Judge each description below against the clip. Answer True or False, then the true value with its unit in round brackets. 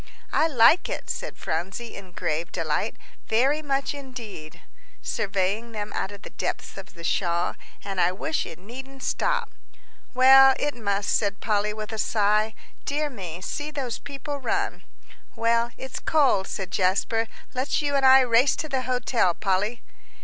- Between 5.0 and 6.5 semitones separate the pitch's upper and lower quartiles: True (5.4 semitones)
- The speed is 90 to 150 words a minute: False (160 wpm)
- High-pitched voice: True (230 Hz)